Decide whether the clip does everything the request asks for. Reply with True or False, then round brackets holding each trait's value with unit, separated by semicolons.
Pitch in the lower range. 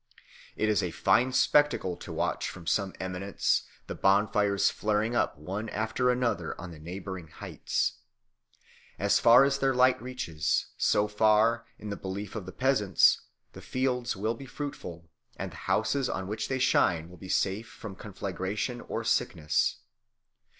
True (105 Hz)